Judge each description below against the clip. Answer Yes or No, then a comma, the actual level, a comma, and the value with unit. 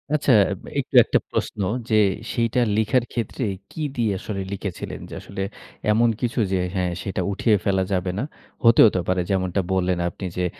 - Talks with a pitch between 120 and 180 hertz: No, low, 100 Hz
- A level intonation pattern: No, average, 3.8 semitones